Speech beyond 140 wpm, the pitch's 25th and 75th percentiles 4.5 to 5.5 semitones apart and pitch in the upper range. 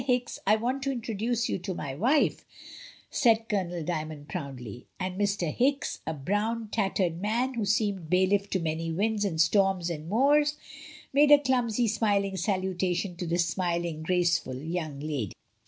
Yes: average, 160 wpm; average, 5.1 semitones; high, 195 Hz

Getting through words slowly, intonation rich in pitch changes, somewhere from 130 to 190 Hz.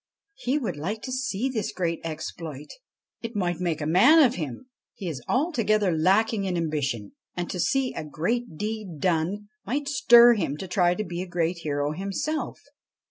No: average, 180 wpm; wide, 6.1 semitones; medium, 185 Hz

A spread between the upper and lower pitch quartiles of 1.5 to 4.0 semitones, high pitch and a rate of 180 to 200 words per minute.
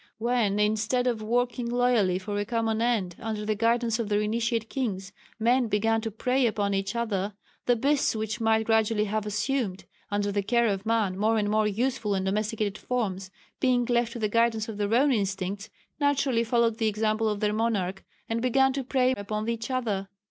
Yes: narrow, 2.4 semitones; high, 220 Hz; average, 190 wpm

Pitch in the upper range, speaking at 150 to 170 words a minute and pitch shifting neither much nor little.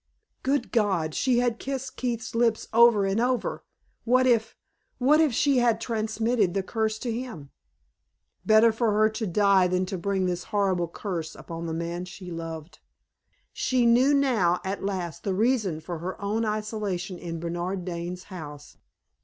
Yes: high, 205 Hz; average, 160 wpm; average, 4.7 semitones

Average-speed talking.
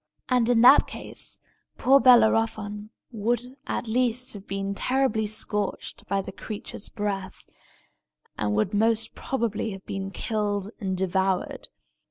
No: slow, 130 wpm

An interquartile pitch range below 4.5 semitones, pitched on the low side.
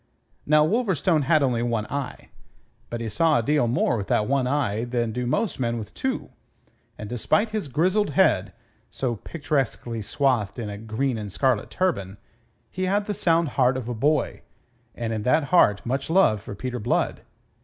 No: average, 5.3 semitones; low, 130 Hz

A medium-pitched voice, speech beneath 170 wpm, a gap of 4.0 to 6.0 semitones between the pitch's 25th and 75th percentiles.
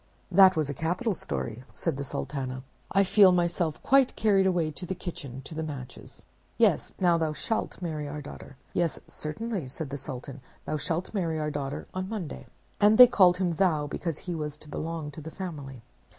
No: medium, 160 Hz; average, 195 wpm; average, 4.3 semitones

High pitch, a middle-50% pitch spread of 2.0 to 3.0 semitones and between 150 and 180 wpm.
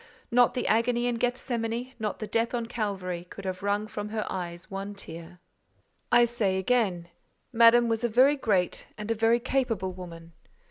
No: high, 220 Hz; average, 4.1 semitones; average, 175 wpm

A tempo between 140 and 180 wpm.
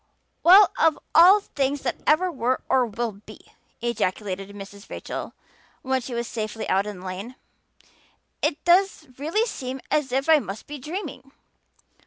Yes: average, 155 wpm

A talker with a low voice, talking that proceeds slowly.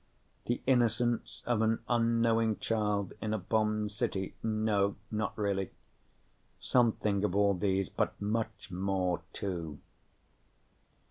Yes: low, 105 Hz; slow, 115 wpm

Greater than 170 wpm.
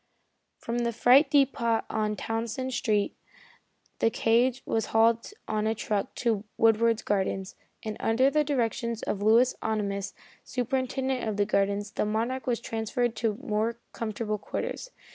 No: average, 145 wpm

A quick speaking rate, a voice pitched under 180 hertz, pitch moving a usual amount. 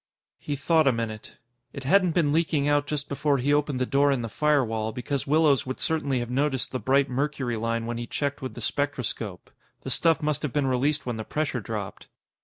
Yes: fast, 210 wpm; medium, 140 Hz; average, 3.4 semitones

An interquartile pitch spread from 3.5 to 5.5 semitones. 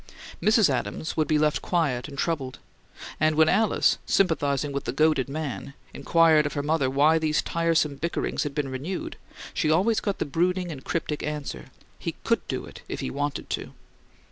No: average, 2.9 semitones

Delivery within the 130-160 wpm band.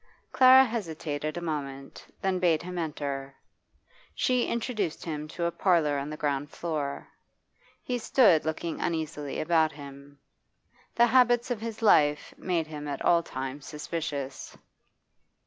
Yes: slow, 135 wpm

